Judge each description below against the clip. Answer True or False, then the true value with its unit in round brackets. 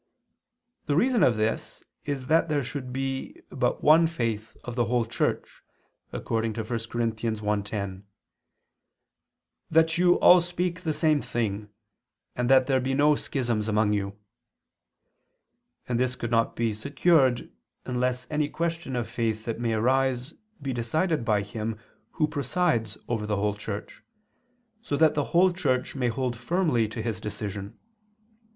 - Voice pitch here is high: False (125 Hz)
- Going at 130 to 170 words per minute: True (150 wpm)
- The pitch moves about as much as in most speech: True (4.9 semitones)